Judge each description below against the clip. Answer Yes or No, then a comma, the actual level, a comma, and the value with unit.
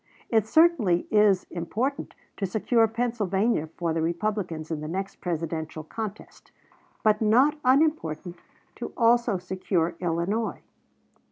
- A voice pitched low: No, high, 195 Hz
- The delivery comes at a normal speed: No, slow, 115 wpm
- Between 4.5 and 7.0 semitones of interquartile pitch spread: Yes, average, 5.0 semitones